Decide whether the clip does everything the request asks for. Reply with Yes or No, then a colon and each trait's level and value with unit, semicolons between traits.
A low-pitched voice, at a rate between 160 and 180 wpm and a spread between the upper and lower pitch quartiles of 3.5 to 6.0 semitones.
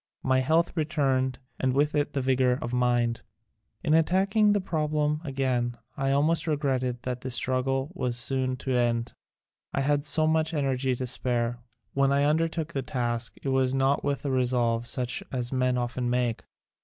No: low, 130 Hz; average, 170 wpm; average, 3.1 semitones